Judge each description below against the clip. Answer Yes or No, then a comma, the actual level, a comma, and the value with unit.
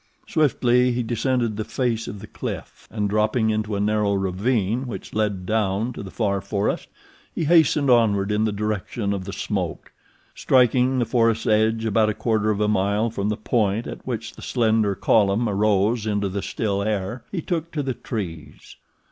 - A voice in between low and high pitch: No, low, 110 Hz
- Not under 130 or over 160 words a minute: No, average, 180 wpm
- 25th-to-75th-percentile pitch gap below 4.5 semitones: Yes, average, 2.7 semitones